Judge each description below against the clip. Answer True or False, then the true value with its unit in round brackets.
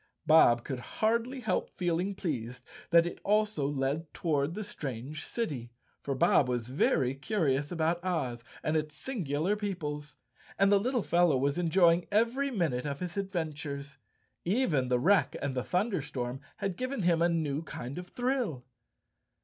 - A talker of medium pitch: True (160 Hz)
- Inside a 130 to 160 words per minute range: True (155 wpm)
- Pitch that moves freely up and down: True (5.9 semitones)